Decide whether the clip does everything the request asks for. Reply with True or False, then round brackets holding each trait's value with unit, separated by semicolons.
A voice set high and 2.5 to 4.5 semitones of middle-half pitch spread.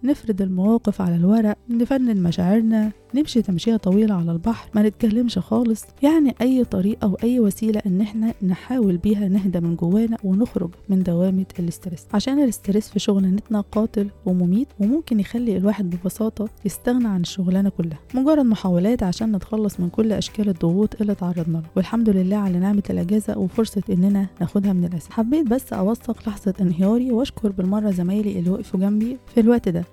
True (210 Hz; 3.2 semitones)